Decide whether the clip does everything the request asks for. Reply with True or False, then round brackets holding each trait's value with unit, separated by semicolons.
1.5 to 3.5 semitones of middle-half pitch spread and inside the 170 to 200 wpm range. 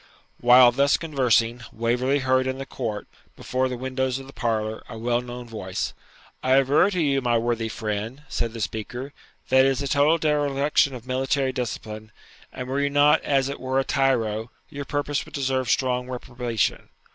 True (2.6 semitones; 180 wpm)